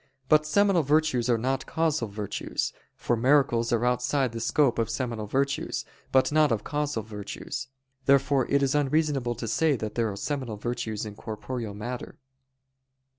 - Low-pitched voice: Yes, low, 125 Hz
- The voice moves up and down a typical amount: Yes, average, 4.1 semitones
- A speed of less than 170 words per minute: Yes, average, 160 wpm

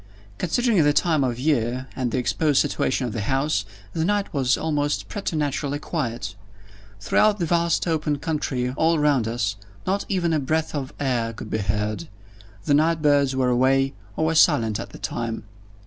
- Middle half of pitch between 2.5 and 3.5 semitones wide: No, average, 4.4 semitones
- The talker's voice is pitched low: No, medium, 145 Hz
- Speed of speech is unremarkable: Yes, average, 175 wpm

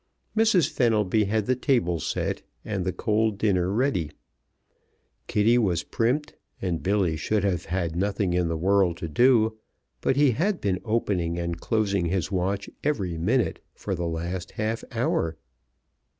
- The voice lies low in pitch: Yes, low, 100 Hz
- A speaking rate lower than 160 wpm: Yes, average, 150 wpm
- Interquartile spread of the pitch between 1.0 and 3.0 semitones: No, average, 4.5 semitones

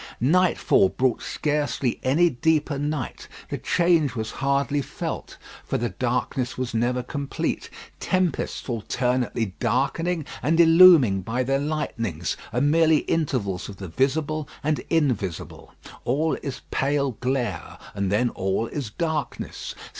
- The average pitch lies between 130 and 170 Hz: Yes, low, 135 Hz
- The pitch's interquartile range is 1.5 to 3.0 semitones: No, average, 4.5 semitones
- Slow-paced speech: Yes, slow, 125 wpm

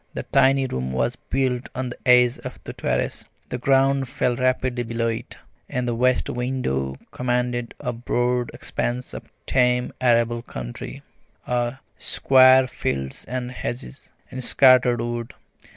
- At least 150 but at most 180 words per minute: No, average, 140 wpm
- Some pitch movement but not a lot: No, narrow, 1.4 semitones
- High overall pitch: No, low, 125 Hz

